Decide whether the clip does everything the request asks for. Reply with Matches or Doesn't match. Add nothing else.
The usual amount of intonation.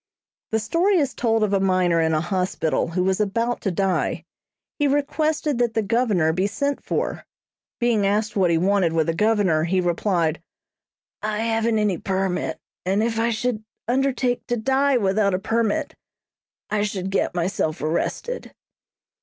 Matches